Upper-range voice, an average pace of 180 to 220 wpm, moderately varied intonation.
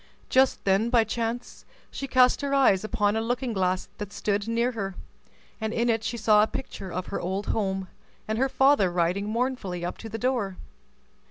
Yes: high, 220 Hz; average, 190 wpm; average, 3.8 semitones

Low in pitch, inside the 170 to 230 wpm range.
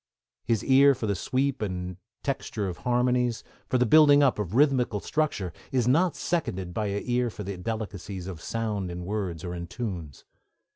Yes: low, 110 Hz; average, 180 wpm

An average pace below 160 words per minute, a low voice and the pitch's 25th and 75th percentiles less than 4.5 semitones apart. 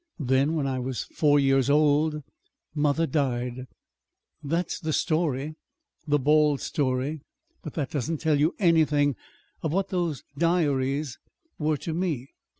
No: average, 140 wpm; medium, 150 Hz; average, 2.7 semitones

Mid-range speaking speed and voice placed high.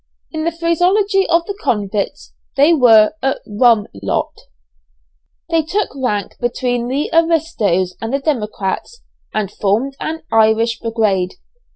No: slow, 130 wpm; high, 245 Hz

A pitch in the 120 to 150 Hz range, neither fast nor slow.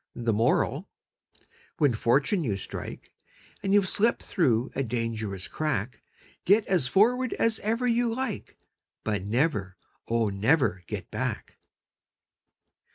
No: low, 135 Hz; slow, 120 wpm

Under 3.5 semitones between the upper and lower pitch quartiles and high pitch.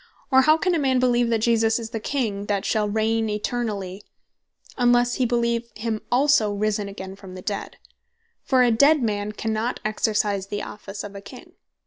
Yes: average, 2.9 semitones; high, 220 Hz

